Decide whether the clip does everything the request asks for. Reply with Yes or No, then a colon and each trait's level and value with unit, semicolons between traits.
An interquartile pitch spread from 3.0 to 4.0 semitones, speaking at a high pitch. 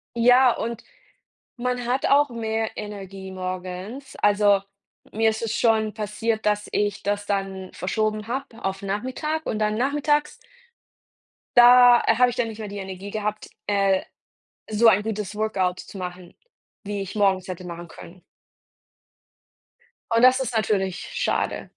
Yes: average, 3.3 semitones; high, 210 Hz